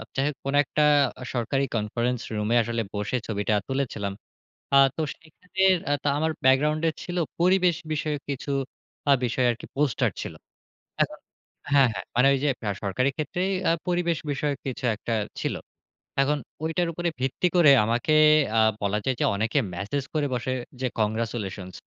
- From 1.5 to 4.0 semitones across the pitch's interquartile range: No, average, 5.0 semitones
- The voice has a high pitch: No, low, 135 Hz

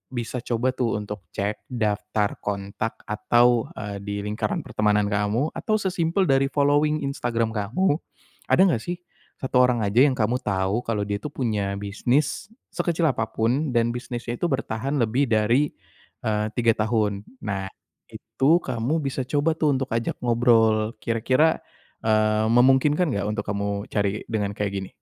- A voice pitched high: No, low, 115 Hz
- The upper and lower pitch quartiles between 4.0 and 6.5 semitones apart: Yes, average, 4.3 semitones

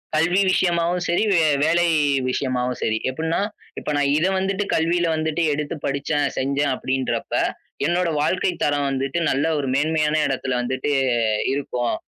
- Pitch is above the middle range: No, medium, 150 Hz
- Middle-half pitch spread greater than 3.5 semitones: Yes, average, 3.9 semitones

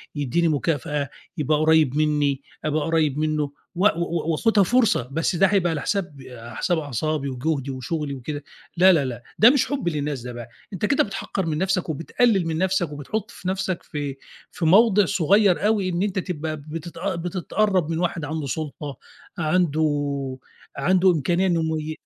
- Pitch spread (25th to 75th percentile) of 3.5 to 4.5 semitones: Yes, average, 4.0 semitones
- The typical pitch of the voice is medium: Yes, medium, 160 Hz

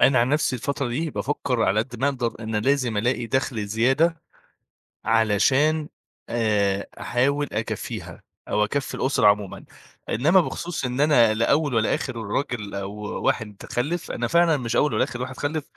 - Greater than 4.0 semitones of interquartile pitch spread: Yes, average, 4.5 semitones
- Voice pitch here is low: Yes, low, 125 Hz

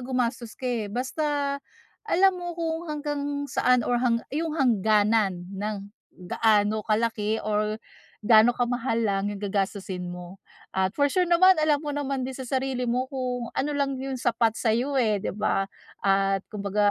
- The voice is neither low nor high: No, high, 235 Hz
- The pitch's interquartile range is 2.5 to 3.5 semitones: No, average, 4.6 semitones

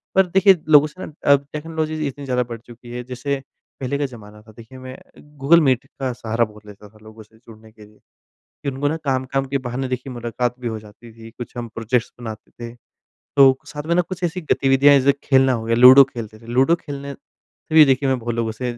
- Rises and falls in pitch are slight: No, average, 3.5 semitones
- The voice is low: Yes, low, 130 Hz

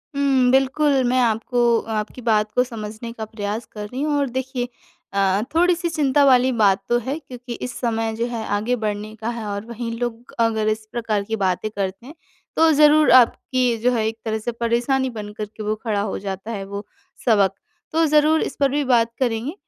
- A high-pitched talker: Yes, high, 235 Hz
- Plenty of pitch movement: No, average, 3.3 semitones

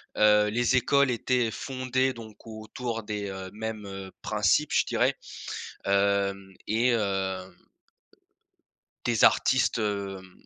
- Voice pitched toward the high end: No, low, 105 Hz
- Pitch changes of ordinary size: Yes, average, 3.5 semitones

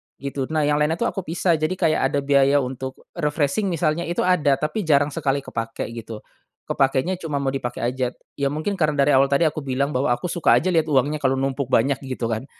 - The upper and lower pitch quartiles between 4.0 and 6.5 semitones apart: No, average, 2.8 semitones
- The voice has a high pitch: No, medium, 140 Hz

